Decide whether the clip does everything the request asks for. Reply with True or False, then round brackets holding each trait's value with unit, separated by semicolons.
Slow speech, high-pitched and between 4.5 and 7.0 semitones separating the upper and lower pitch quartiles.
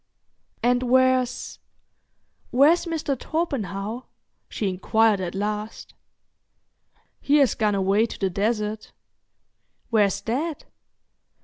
False (90 wpm; 225 Hz; 4.1 semitones)